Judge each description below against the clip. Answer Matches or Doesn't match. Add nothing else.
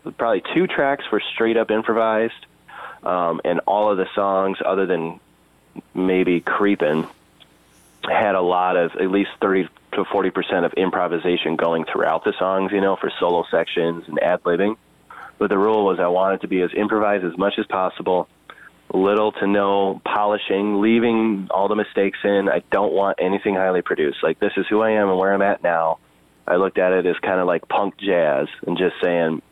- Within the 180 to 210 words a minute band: Matches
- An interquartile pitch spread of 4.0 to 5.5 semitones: Doesn't match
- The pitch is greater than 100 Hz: Doesn't match